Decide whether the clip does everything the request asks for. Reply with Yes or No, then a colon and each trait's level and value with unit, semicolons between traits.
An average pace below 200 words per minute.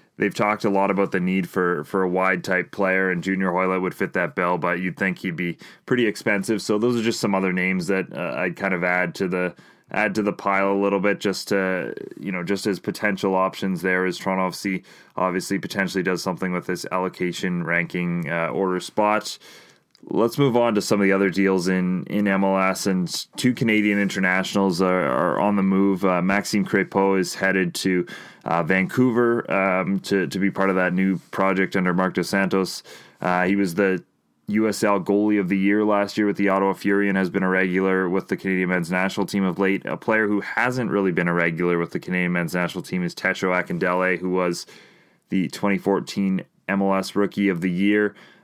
No: fast, 205 wpm